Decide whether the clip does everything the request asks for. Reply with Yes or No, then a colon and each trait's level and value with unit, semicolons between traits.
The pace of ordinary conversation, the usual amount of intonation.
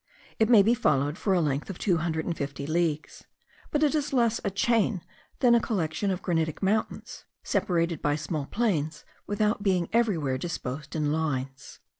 No: average, 175 wpm; wide, 6.0 semitones